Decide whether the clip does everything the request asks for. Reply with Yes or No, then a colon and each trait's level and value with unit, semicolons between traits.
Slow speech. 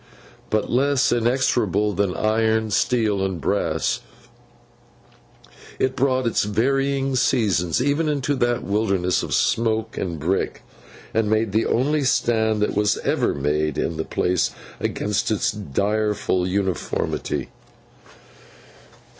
Yes: slow, 115 wpm